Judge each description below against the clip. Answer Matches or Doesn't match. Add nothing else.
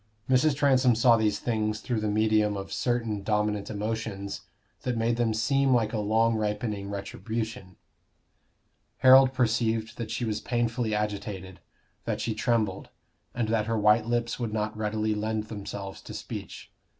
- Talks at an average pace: Matches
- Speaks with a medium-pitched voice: Doesn't match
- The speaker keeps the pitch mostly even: Matches